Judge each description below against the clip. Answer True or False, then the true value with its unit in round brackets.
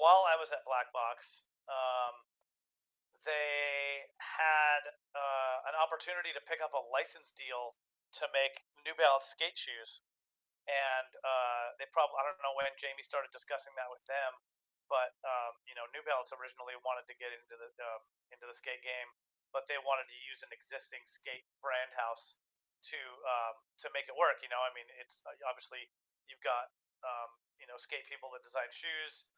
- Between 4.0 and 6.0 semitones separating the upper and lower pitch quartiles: False (2.6 semitones)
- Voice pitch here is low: True (130 Hz)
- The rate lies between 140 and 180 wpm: True (175 wpm)